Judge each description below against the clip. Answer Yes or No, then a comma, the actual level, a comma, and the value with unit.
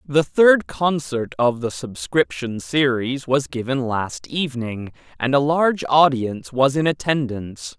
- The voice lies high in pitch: No, low, 135 Hz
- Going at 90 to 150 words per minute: Yes, average, 140 wpm